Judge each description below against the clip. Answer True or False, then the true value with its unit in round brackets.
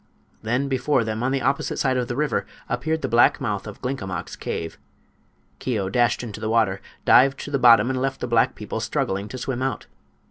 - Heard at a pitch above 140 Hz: False (120 Hz)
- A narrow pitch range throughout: False (3.5 semitones)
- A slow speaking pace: False (205 wpm)